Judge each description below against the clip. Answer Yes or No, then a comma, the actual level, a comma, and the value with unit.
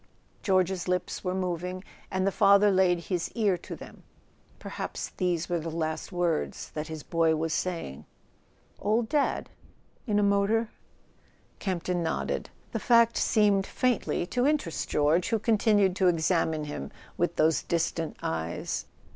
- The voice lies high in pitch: No, medium, 180 Hz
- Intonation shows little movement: No, average, 3.6 semitones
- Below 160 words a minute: Yes, average, 140 wpm